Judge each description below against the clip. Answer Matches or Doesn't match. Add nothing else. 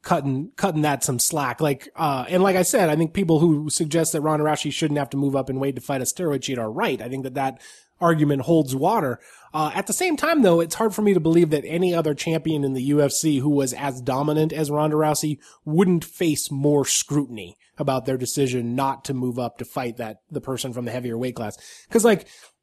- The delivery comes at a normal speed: Doesn't match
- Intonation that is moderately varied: Matches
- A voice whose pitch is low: Doesn't match